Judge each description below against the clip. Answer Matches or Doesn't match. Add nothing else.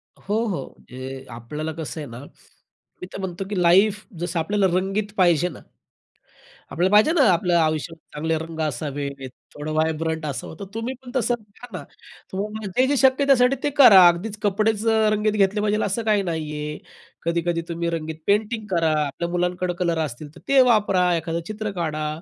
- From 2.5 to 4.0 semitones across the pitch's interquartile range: Doesn't match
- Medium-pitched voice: Matches